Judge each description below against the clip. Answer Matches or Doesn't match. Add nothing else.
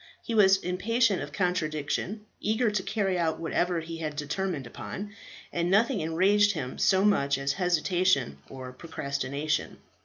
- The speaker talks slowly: Doesn't match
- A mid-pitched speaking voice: Matches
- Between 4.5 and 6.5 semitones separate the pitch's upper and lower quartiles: Matches